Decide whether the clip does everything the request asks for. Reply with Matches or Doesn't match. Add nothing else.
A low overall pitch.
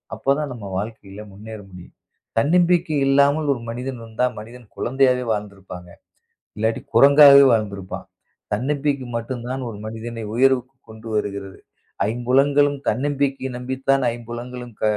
Matches